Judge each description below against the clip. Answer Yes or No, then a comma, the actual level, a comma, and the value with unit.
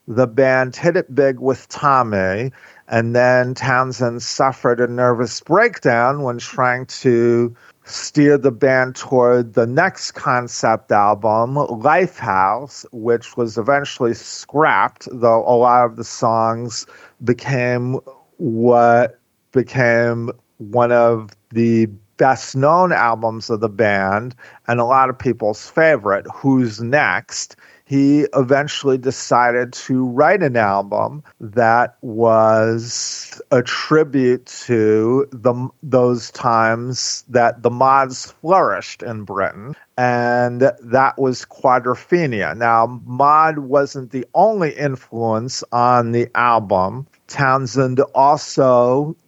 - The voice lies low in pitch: Yes, low, 125 Hz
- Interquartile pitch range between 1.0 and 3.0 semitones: Yes, narrow, 2.5 semitones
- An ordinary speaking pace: No, slow, 110 wpm